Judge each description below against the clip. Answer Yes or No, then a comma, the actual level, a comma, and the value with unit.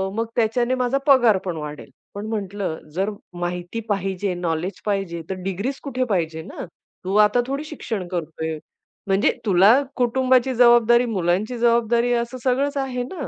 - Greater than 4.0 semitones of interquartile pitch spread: Yes, average, 5.1 semitones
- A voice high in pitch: Yes, high, 215 Hz